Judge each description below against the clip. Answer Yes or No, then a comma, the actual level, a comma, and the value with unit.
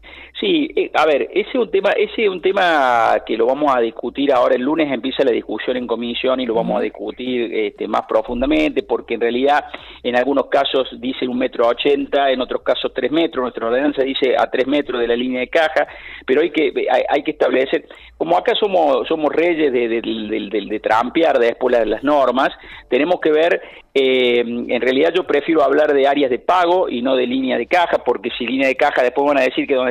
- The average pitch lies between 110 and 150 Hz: Yes, medium, 140 Hz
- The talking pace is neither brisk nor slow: No, fast, 225 wpm